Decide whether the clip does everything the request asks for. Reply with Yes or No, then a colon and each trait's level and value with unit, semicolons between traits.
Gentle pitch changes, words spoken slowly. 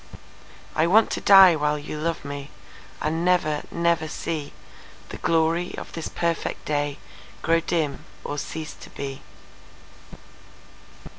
Yes: narrow, 2.3 semitones; slow, 115 wpm